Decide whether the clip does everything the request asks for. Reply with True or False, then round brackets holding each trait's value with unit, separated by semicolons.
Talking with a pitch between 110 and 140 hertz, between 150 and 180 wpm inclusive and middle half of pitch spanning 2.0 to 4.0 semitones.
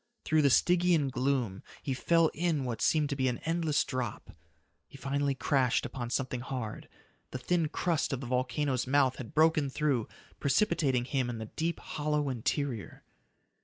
True (135 Hz; 165 wpm; 3.3 semitones)